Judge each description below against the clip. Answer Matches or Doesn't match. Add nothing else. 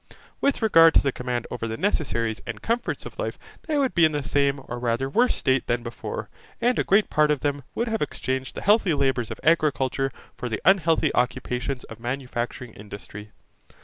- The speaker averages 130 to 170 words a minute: Doesn't match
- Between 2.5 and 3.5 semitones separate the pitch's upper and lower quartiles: Doesn't match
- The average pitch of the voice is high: Doesn't match